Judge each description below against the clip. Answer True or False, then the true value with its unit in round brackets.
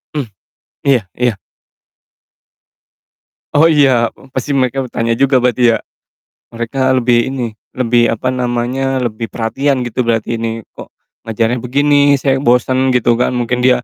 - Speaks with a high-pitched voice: False (125 Hz)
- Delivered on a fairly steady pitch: True (2.2 semitones)